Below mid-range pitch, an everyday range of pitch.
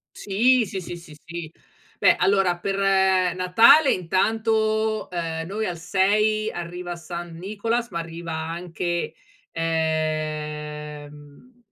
No: medium, 175 Hz; average, 4.6 semitones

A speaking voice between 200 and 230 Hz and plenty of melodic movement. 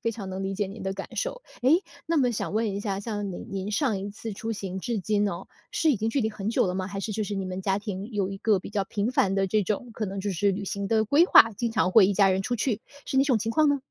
No: high, 205 Hz; average, 2.7 semitones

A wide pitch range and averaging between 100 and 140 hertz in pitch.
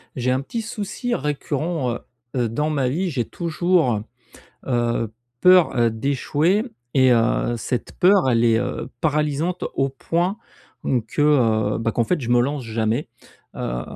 Yes: wide, 5.8 semitones; low, 135 Hz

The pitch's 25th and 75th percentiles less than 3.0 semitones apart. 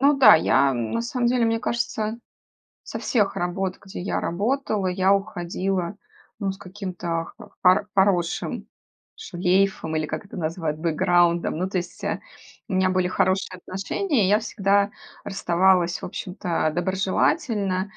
Yes: narrow, 2.6 semitones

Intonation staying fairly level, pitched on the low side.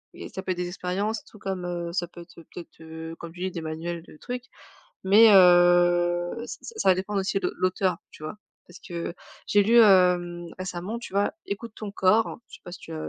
No: narrow, 2.1 semitones; medium, 180 Hz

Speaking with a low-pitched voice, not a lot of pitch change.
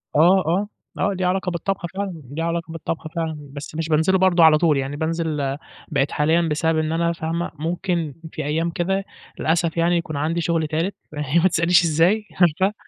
No: medium, 165 Hz; narrow, 2.0 semitones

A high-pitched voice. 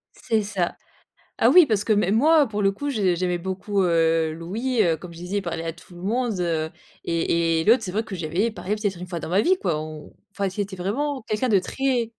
Yes: high, 195 Hz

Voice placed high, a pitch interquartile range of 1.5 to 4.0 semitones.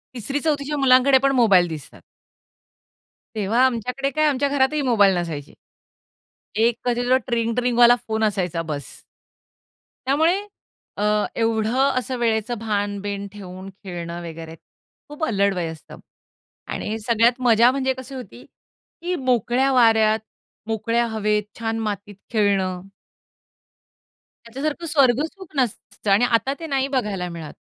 No: high, 230 Hz; average, 4.6 semitones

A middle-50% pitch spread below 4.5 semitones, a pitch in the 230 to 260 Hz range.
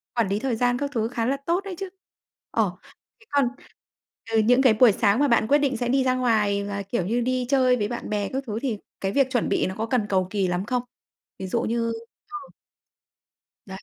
Yes: average, 3.8 semitones; high, 235 Hz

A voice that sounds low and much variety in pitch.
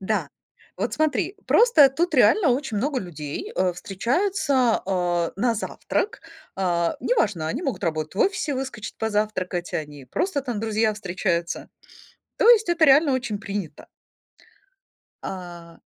No: high, 215 Hz; wide, 7.9 semitones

